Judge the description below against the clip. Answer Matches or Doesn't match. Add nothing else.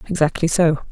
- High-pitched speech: Doesn't match